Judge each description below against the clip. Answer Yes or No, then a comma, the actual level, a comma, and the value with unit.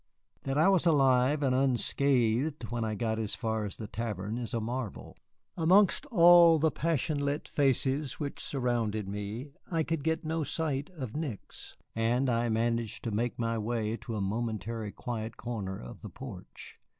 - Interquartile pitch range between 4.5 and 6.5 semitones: Yes, average, 4.8 semitones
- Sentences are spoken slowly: No, average, 170 wpm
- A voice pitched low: Yes, low, 120 Hz